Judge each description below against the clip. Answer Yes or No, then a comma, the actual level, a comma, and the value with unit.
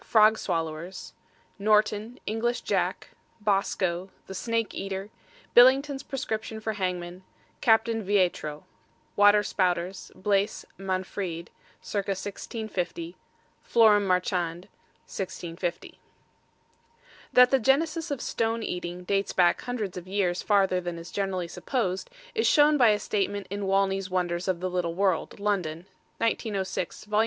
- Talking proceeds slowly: Yes, slow, 120 wpm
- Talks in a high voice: Yes, high, 195 Hz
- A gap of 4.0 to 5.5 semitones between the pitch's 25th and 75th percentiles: No, average, 3.3 semitones